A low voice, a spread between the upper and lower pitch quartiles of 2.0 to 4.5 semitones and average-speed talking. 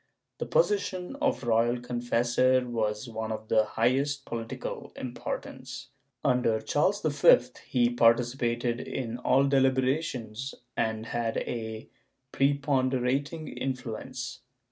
No: low, 125 Hz; average, 2.8 semitones; slow, 110 wpm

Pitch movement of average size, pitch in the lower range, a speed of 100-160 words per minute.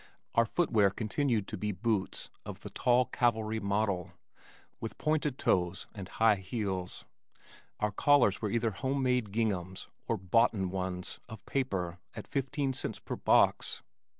Yes: average, 4.2 semitones; low, 110 Hz; average, 145 wpm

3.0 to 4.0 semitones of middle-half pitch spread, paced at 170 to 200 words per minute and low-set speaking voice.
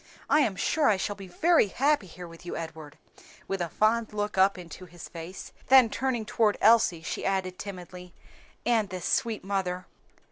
No: average, 3.7 semitones; average, 180 wpm; high, 195 Hz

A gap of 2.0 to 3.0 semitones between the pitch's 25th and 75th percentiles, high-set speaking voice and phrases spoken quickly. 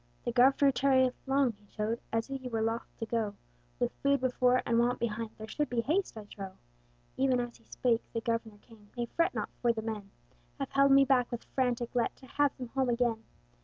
Yes: narrow, 2.6 semitones; high, 240 Hz; fast, 215 wpm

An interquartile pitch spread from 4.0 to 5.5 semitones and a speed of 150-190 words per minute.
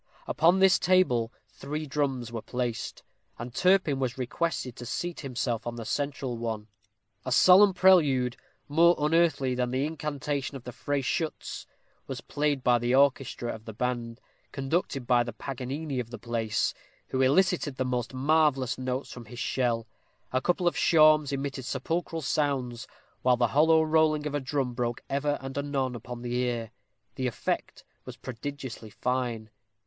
No: average, 3.5 semitones; average, 160 wpm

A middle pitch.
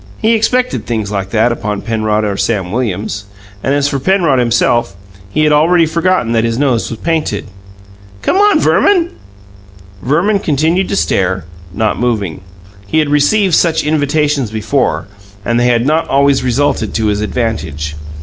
No: low, 125 Hz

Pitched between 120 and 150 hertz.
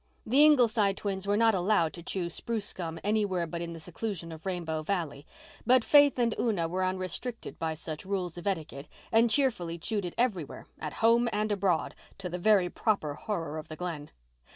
No: medium, 185 Hz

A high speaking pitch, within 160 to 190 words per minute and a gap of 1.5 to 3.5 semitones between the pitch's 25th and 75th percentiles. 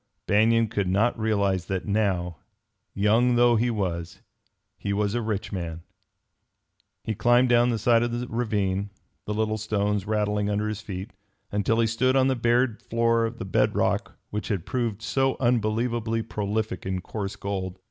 No: low, 110 Hz; average, 170 wpm; average, 2.7 semitones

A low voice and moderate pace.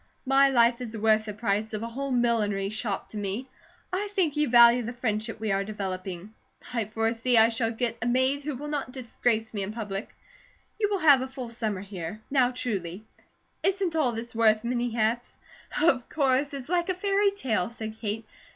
No: high, 235 Hz; average, 195 wpm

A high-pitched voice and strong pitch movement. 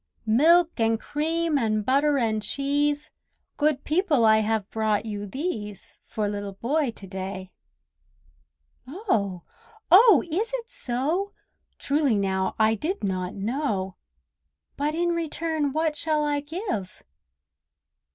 Yes: very high, 275 Hz; wide, 7.0 semitones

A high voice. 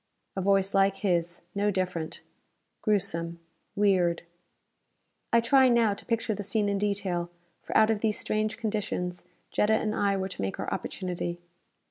Yes: high, 200 Hz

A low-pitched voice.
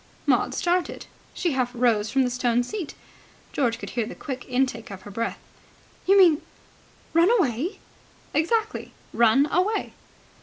No: very high, 265 Hz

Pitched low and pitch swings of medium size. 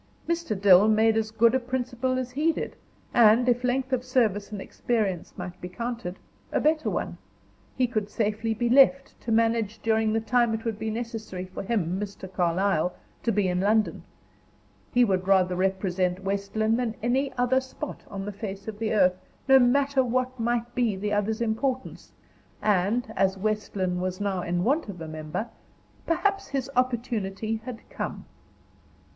No: high, 220 Hz; average, 4.0 semitones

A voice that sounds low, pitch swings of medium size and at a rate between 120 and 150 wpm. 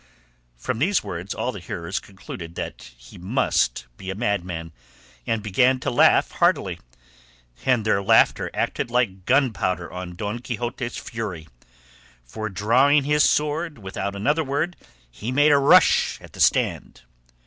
No: low, 110 Hz; wide, 6.0 semitones; average, 145 wpm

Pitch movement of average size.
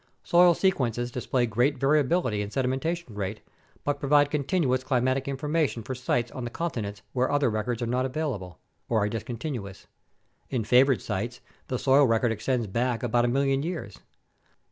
Yes: average, 3.5 semitones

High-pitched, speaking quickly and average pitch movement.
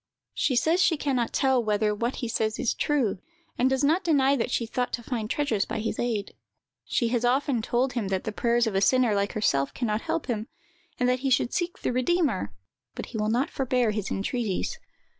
Yes: high, 240 Hz; fast, 220 wpm; average, 3.6 semitones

